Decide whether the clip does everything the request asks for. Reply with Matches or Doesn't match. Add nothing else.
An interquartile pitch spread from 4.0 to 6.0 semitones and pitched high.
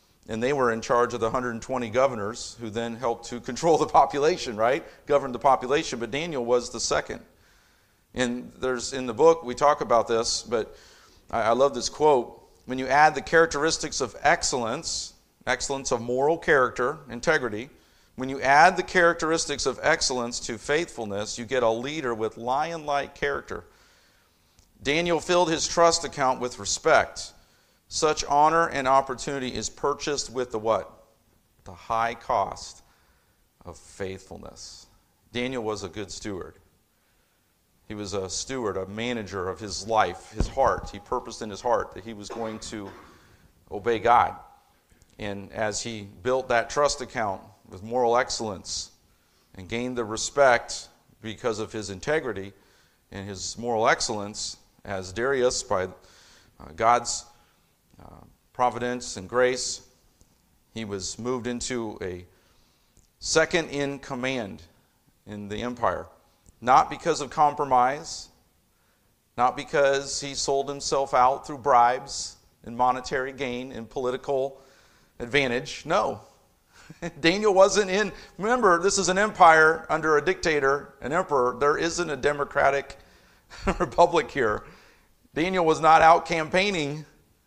Doesn't match